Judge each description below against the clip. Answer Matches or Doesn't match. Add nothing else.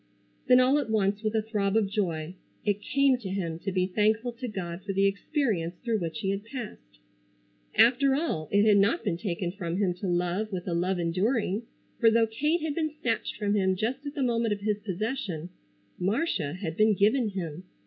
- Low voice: Doesn't match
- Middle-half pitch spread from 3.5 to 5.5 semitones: Matches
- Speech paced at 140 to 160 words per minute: Doesn't match